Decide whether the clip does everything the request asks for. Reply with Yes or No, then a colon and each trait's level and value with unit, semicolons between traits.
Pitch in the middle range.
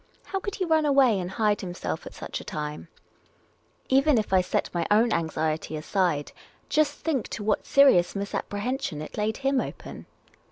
No: high, 210 Hz